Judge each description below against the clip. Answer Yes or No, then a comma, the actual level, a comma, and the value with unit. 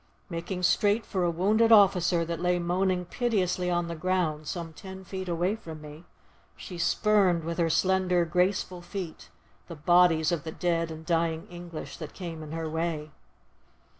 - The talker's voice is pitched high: No, medium, 175 Hz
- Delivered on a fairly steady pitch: Yes, narrow, 2.2 semitones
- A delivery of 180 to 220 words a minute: No, average, 165 wpm